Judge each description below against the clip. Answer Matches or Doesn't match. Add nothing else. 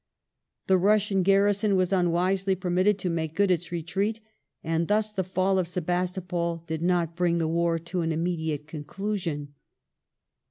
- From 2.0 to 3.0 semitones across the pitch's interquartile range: Matches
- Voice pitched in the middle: Matches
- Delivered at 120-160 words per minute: Matches